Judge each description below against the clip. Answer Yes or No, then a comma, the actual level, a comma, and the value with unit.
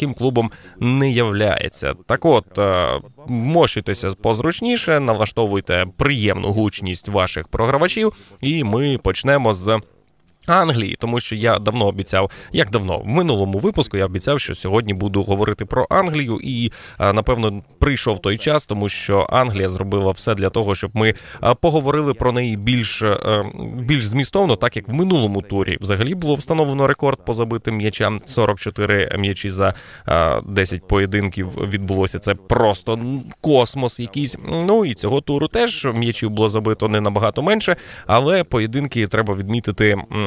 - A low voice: Yes, low, 110 Hz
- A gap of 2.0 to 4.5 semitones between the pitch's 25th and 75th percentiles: No, average, 5.2 semitones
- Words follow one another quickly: No, average, 140 wpm